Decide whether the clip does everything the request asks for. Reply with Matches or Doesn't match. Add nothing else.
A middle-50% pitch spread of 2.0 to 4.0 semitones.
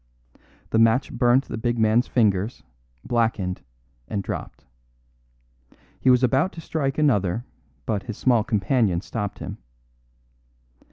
Matches